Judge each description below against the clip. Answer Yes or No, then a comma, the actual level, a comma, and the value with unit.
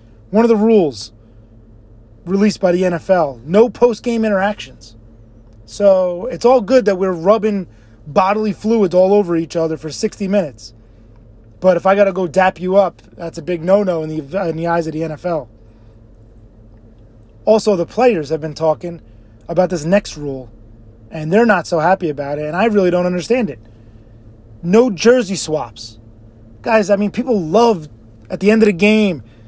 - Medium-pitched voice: Yes, medium, 170 Hz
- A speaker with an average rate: Yes, average, 175 wpm